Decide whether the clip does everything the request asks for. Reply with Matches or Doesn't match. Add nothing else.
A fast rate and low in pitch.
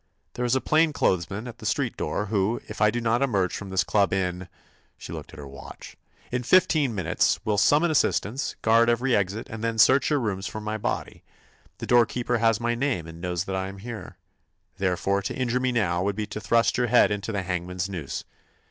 Matches